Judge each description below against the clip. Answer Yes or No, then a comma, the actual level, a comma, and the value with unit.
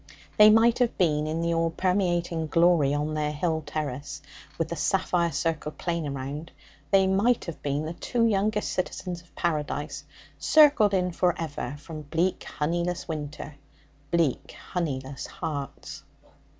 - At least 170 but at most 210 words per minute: No, average, 145 wpm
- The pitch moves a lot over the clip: No, average, 3.4 semitones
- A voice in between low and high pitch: Yes, medium, 165 Hz